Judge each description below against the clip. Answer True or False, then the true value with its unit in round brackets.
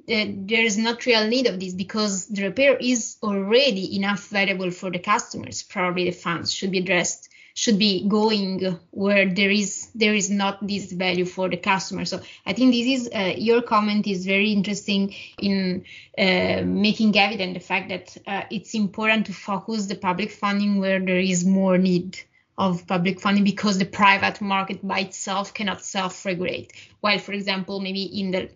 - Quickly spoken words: True (180 wpm)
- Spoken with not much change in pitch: True (2.0 semitones)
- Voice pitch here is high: True (195 Hz)